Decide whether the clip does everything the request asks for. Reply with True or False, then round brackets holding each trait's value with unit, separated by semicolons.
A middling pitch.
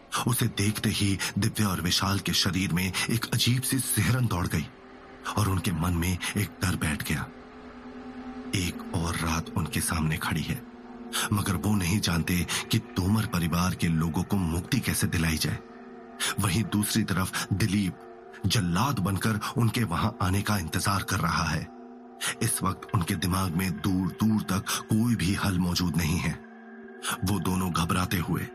False (100 Hz)